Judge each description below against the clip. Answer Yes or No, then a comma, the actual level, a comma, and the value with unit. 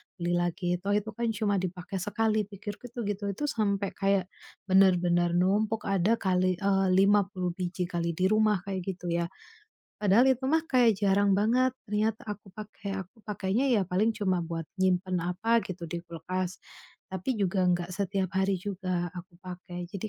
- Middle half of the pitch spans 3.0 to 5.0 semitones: No, narrow, 2.6 semitones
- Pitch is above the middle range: Yes, high, 195 Hz